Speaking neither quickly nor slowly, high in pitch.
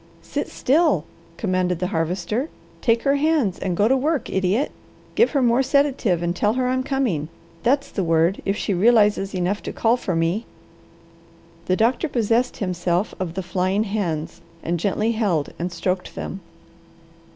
Yes: average, 160 wpm; high, 205 Hz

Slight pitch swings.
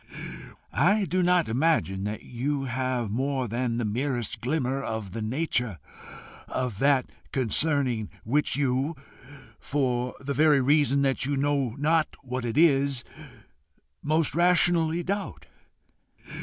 No: average, 3.8 semitones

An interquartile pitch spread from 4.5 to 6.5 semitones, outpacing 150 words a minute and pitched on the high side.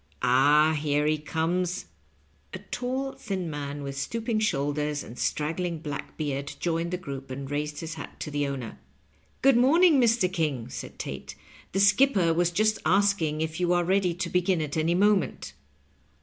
No: average, 4.8 semitones; average, 180 wpm; medium, 165 Hz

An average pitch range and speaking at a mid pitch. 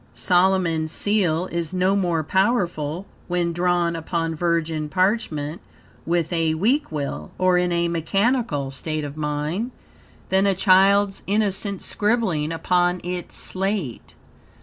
Yes: average, 3.2 semitones; medium, 175 Hz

